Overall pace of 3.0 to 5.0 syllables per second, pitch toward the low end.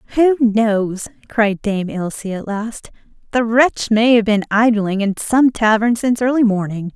No: 4.2 syllables/s; high, 220 Hz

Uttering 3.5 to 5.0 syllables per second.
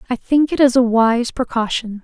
Yes: 4.9 syllables/s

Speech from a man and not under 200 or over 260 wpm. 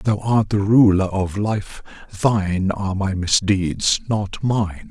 No: male; average, 160 wpm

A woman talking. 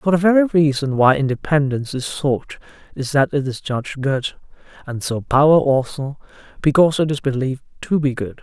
No: male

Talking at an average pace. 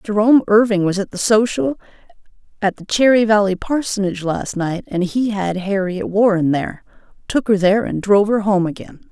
Yes: average, 170 wpm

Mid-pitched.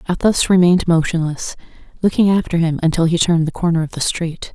Yes: medium, 170 Hz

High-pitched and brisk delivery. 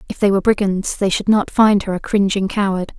Yes: high, 200 Hz; fast, 240 wpm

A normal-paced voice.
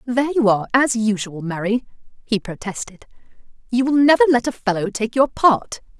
Yes: average, 170 wpm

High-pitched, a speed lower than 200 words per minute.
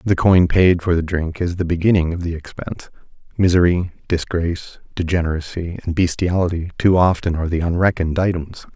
No: very low, 85 Hz; average, 160 wpm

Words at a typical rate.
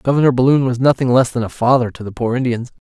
No: fast, 245 wpm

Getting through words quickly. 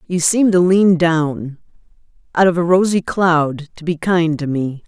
No: average, 160 wpm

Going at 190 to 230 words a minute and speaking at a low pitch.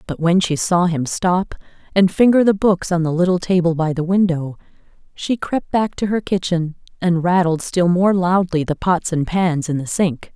No: average, 195 wpm; medium, 175 Hz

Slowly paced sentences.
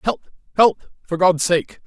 No: average, 160 wpm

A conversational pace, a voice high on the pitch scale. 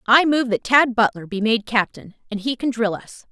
No: fast, 235 wpm; high, 230 Hz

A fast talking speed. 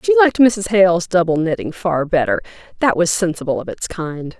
No: average, 190 wpm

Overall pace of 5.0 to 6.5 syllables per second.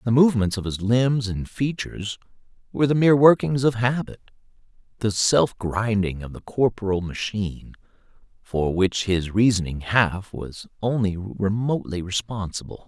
No: 4.8 syllables/s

